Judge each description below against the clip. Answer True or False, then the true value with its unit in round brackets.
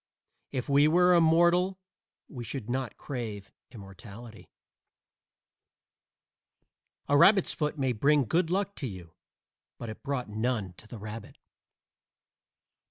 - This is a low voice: True (130 Hz)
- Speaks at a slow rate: True (115 wpm)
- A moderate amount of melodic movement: False (6.5 semitones)